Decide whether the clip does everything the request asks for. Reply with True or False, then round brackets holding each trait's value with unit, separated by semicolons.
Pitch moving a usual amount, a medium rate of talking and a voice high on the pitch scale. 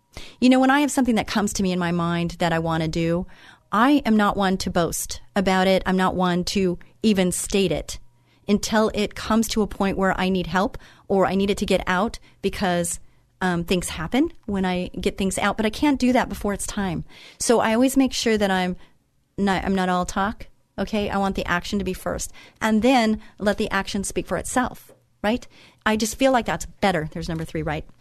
False (3.0 semitones; 225 wpm; 195 Hz)